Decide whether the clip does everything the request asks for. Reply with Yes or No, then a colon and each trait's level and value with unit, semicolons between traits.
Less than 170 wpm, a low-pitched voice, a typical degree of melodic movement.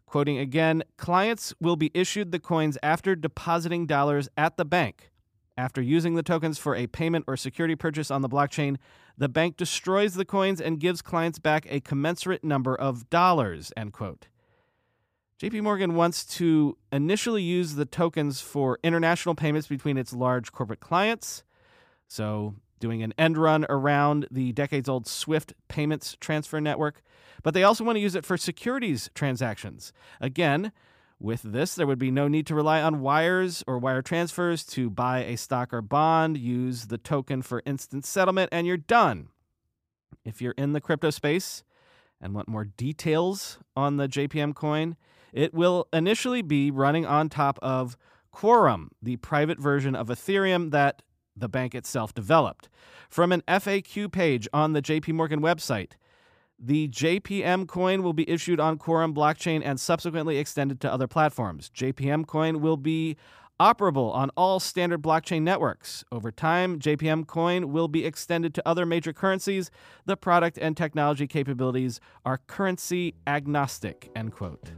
No: average, 160 wpm; medium, 155 Hz; average, 4.3 semitones